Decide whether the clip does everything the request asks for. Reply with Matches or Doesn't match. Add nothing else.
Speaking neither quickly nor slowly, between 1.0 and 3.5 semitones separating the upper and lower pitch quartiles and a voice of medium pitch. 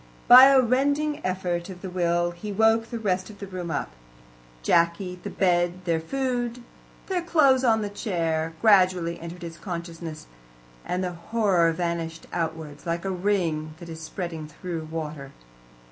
Doesn't match